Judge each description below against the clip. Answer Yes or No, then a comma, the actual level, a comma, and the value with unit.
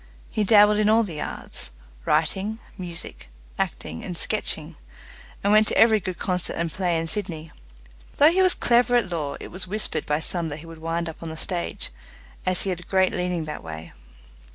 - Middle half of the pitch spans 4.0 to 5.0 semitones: Yes, average, 4.4 semitones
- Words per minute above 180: Yes, average, 200 wpm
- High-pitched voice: No, medium, 180 Hz